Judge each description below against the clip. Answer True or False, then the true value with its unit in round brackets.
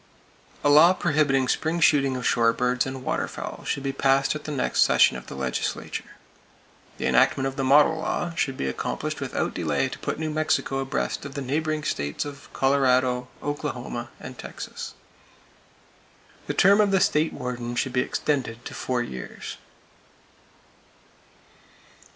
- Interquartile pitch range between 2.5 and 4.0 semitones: True (3.2 semitones)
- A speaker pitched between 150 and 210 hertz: False (135 Hz)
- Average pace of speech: True (155 wpm)